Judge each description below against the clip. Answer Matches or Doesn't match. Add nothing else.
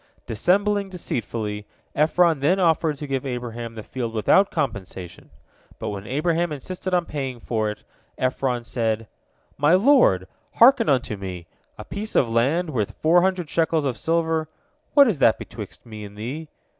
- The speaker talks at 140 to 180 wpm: Matches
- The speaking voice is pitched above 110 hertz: Matches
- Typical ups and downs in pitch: Doesn't match